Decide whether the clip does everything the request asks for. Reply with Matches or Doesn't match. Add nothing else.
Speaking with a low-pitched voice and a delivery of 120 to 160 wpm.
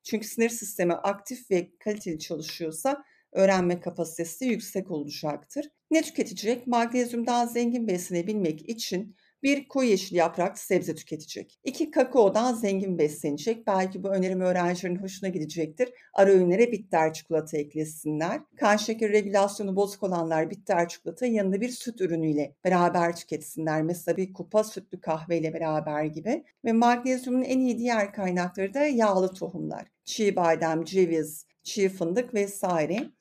Doesn't match